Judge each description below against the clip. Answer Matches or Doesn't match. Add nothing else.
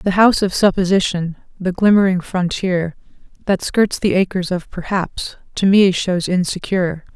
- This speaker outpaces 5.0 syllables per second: Doesn't match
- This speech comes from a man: Doesn't match